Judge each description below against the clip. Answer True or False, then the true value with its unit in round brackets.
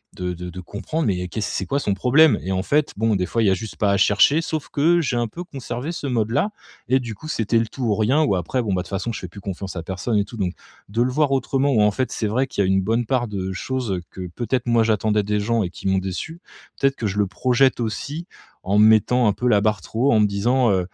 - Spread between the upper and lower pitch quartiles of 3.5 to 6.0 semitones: True (4.6 semitones)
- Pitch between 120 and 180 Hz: False (110 Hz)